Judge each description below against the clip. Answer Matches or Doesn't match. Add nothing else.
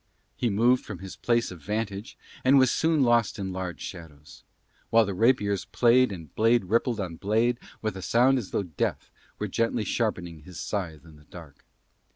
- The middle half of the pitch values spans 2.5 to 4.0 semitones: Doesn't match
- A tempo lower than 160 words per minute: Doesn't match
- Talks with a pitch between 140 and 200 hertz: Doesn't match